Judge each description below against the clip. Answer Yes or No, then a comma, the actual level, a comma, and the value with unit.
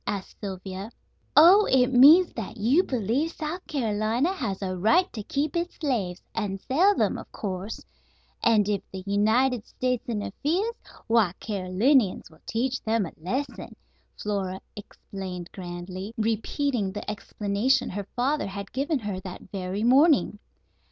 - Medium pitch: No, high, 220 Hz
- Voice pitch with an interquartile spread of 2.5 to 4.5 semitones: No, wide, 5.4 semitones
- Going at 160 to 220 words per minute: No, average, 140 wpm